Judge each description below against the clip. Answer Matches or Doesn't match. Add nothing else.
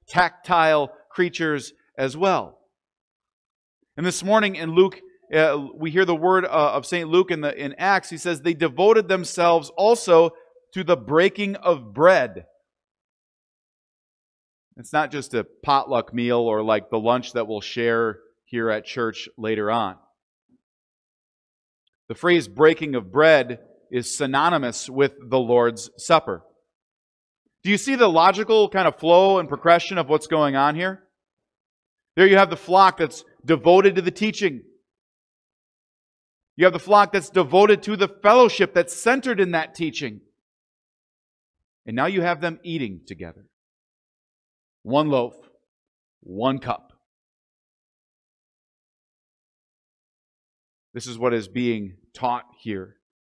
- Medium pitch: Matches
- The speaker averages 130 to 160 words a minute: Matches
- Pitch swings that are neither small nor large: Doesn't match